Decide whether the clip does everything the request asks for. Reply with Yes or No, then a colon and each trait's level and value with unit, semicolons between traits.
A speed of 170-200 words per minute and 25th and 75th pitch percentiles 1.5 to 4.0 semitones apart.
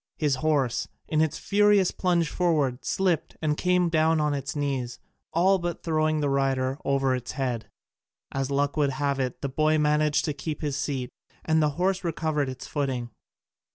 Yes: average, 175 wpm; average, 2.9 semitones